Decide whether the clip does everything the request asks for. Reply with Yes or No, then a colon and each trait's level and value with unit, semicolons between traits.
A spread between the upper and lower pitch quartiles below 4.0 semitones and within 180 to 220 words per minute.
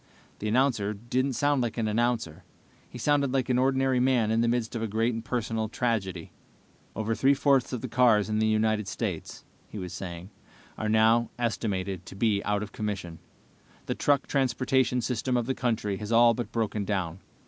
Yes: average, 3.0 semitones; average, 190 wpm